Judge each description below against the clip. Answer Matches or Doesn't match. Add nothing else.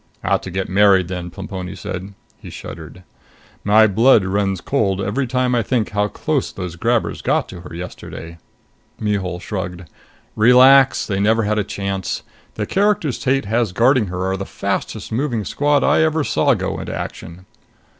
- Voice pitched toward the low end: Matches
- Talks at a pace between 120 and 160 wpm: Doesn't match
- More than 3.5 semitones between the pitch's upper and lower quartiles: Matches